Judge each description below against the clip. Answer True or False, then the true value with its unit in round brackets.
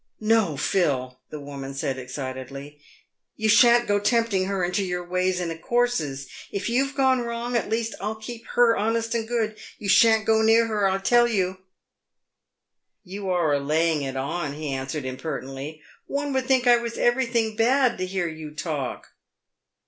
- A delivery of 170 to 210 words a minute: True (175 wpm)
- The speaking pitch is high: True (195 Hz)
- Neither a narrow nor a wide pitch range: False (7.5 semitones)